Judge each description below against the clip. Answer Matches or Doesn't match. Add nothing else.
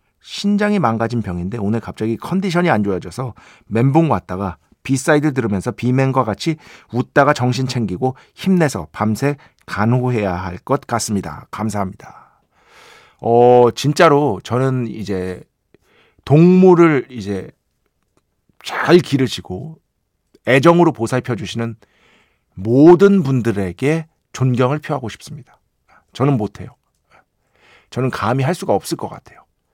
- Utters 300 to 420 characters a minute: Doesn't match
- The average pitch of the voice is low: Matches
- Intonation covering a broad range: Matches